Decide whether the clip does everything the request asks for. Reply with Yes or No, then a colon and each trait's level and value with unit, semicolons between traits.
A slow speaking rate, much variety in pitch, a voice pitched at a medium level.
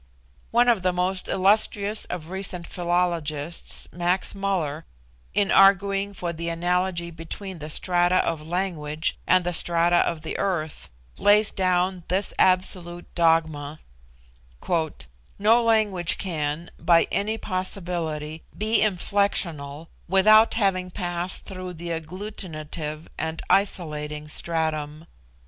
No: slow, 115 wpm; average, 3.0 semitones; medium, 175 Hz